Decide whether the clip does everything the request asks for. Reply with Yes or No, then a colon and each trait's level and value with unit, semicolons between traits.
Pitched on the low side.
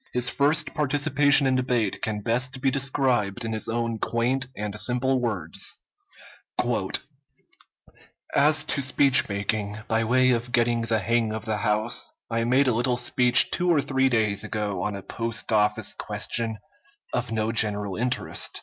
Yes: low, 120 Hz